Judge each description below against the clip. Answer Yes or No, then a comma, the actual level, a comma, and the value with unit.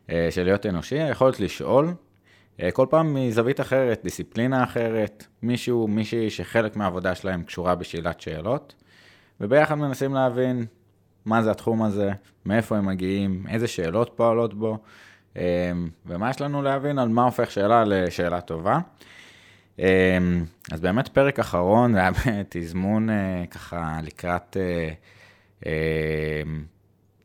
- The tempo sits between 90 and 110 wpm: No, average, 130 wpm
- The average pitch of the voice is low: Yes, low, 100 Hz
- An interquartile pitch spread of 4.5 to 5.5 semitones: Yes, average, 4.8 semitones